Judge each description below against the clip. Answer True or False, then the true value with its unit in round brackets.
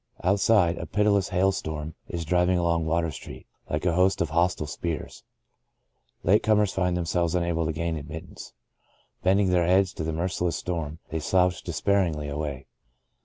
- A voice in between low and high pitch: False (85 Hz)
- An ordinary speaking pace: True (165 wpm)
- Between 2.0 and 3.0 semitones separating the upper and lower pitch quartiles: True (2.5 semitones)